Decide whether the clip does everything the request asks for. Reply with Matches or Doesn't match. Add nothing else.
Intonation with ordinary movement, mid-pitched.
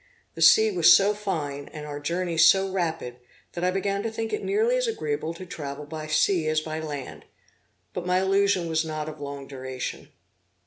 Matches